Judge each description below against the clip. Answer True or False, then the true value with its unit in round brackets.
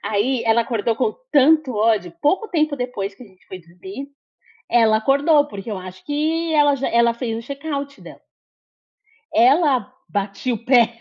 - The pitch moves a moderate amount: True (4.9 semitones)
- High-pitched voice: True (245 Hz)